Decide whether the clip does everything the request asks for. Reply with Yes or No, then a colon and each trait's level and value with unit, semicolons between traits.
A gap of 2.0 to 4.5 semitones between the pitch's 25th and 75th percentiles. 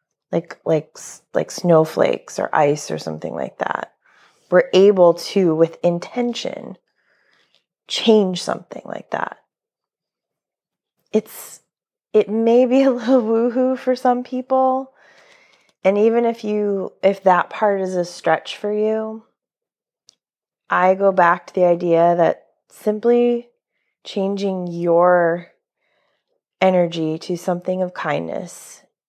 No: average, 5.1 semitones